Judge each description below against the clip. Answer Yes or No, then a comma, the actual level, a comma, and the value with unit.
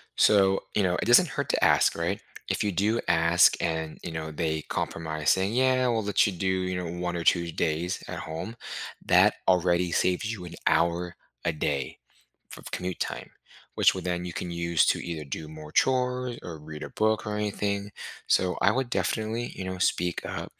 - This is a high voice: No, very low, 90 Hz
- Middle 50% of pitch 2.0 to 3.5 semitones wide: No, average, 3.9 semitones